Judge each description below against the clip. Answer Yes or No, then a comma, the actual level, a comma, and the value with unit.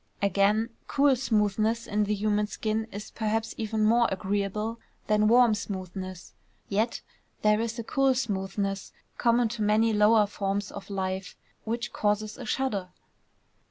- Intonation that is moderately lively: No, narrow, 2.2 semitones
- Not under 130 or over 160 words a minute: Yes, average, 140 wpm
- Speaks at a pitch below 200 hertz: No, high, 215 Hz